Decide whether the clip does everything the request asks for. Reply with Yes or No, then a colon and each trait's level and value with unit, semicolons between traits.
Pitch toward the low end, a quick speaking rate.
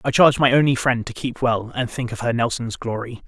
Yes: low, 120 Hz; fast, 255 wpm